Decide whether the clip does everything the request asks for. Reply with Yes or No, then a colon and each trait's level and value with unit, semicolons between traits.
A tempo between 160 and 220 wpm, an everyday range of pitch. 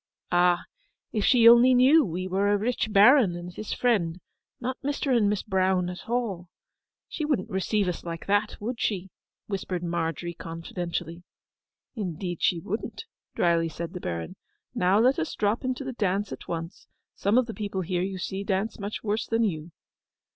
Yes: average, 175 wpm; average, 4.4 semitones